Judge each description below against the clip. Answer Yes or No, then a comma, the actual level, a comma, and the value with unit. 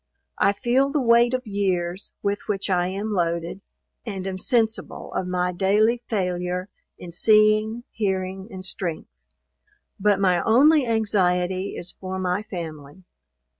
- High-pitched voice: Yes, high, 195 Hz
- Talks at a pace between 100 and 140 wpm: Yes, slow, 135 wpm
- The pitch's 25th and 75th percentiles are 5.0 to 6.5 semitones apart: No, average, 3.2 semitones